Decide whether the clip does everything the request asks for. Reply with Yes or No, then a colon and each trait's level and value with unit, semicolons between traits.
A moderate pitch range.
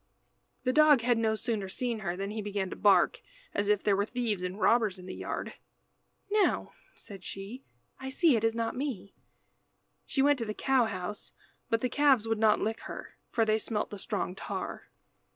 Yes: average, 3.6 semitones